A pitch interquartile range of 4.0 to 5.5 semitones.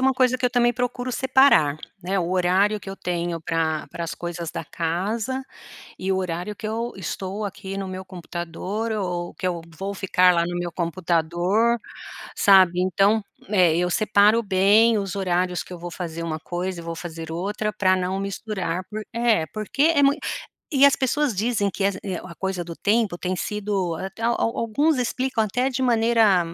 Yes: average, 4.3 semitones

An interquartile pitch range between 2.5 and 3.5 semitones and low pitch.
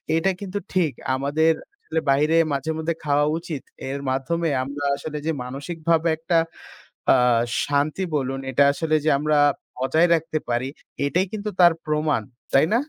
No: average, 2.8 semitones; medium, 155 Hz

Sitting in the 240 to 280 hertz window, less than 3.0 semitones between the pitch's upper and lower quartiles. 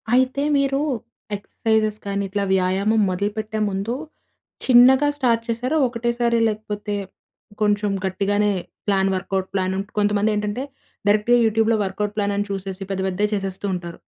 No: high, 210 Hz; narrow, 2.5 semitones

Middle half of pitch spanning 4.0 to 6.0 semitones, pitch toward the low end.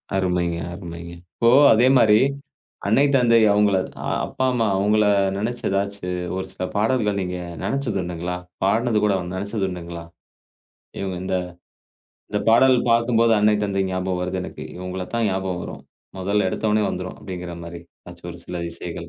No: average, 3.3 semitones; very low, 95 Hz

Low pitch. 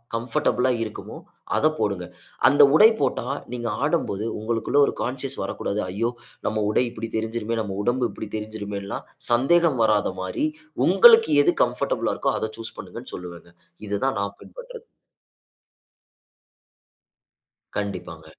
Yes: low, 115 Hz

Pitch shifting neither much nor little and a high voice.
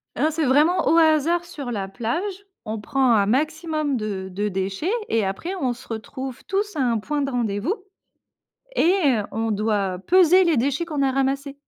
No: wide, 6.4 semitones; very high, 270 Hz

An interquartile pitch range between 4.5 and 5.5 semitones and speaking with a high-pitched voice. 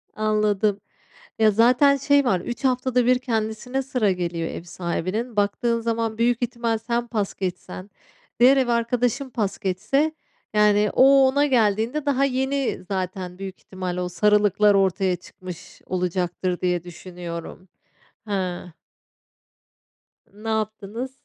Yes: average, 4.9 semitones; high, 215 Hz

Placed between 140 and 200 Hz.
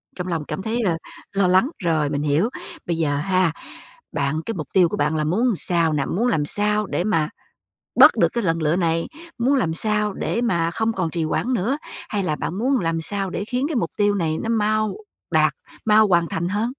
Yes: medium, 185 Hz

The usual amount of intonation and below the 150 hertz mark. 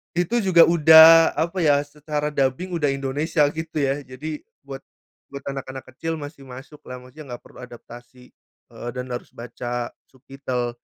Yes: average, 3.8 semitones; medium, 140 Hz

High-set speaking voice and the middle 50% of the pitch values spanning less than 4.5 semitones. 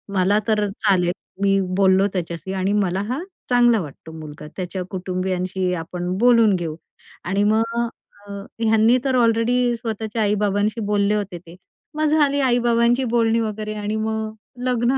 Yes: high, 210 Hz; average, 3.7 semitones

